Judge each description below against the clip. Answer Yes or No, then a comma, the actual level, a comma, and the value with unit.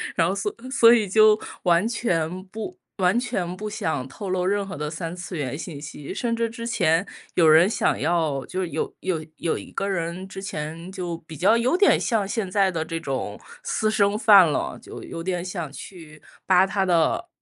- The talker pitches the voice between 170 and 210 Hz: Yes, medium, 185 Hz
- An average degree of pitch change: Yes, average, 3.9 semitones